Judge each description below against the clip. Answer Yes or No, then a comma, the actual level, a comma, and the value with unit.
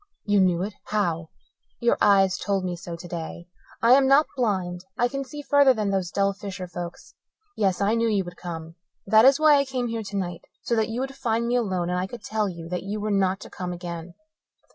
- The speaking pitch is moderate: No, high, 200 Hz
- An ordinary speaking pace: No, fast, 225 wpm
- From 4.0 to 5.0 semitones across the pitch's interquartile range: Yes, average, 4.6 semitones